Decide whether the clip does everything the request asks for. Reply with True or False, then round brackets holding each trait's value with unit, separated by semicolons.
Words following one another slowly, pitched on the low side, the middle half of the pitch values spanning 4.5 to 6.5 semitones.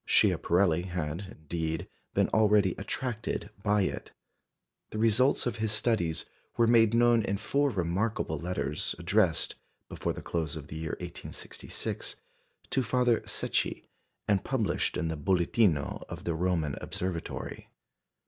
True (130 wpm; 95 Hz; 5.3 semitones)